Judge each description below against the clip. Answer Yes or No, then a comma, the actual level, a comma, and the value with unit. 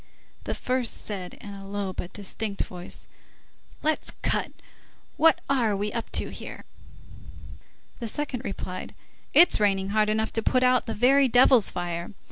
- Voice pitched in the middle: No, high, 215 Hz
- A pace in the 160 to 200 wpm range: No, average, 150 wpm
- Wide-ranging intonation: No, average, 4.3 semitones